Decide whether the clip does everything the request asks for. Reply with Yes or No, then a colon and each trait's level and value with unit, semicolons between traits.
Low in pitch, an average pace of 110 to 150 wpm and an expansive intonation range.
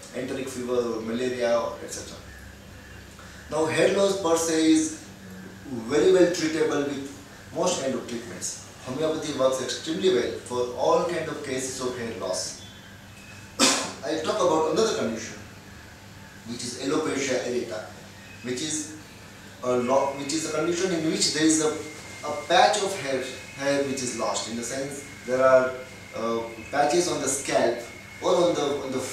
Yes: low, 125 Hz; average, 140 wpm; wide, 6.7 semitones